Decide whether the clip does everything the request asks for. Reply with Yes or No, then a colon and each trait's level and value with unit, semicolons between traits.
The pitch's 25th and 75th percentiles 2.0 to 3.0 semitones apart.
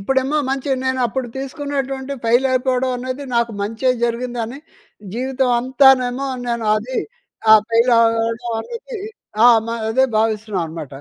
Yes: narrow, 2.6 semitones